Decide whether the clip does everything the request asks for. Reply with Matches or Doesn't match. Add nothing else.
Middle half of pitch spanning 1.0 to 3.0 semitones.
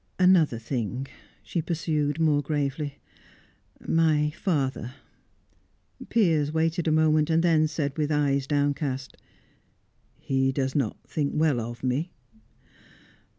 Matches